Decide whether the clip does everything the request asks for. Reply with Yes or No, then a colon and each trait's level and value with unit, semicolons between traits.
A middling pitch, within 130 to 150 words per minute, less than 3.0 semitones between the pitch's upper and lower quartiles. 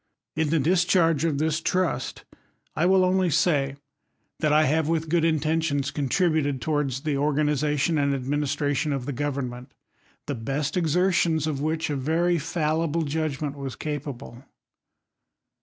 Yes: medium, 150 Hz; average, 145 wpm; narrow, 2.5 semitones